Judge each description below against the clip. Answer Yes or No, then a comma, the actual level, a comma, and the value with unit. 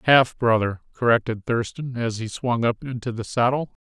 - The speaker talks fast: No, average, 170 wpm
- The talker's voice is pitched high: No, low, 120 Hz